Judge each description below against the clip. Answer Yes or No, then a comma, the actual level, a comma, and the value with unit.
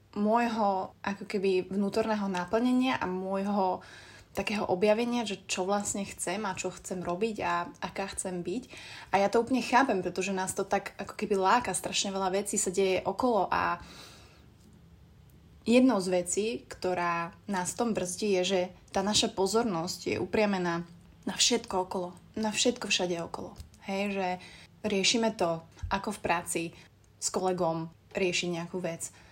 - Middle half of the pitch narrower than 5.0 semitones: Yes, average, 2.8 semitones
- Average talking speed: Yes, average, 150 wpm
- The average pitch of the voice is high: Yes, high, 195 Hz